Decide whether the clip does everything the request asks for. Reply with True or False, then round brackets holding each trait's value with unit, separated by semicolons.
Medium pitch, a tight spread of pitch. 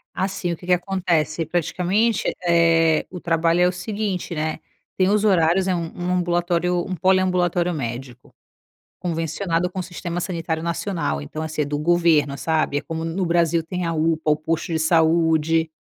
True (170 Hz; 2.0 semitones)